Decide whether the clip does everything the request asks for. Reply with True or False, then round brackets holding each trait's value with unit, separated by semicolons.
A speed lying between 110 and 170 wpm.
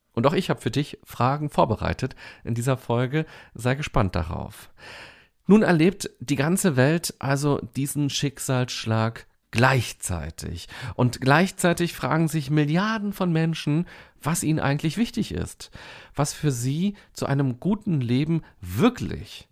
True (130 wpm)